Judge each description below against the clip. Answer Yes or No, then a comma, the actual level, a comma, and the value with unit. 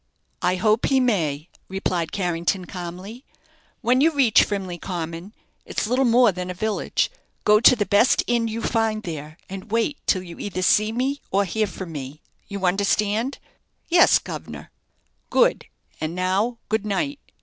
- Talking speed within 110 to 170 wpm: Yes, average, 160 wpm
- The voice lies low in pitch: No, high, 205 Hz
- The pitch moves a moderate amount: Yes, average, 4.2 semitones